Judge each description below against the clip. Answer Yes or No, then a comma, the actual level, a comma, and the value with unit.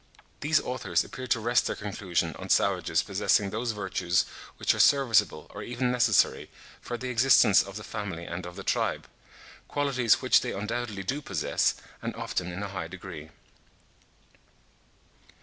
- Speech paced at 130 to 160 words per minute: Yes, average, 150 wpm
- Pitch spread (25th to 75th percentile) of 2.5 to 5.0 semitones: Yes, average, 4.6 semitones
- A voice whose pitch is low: Yes, low, 105 Hz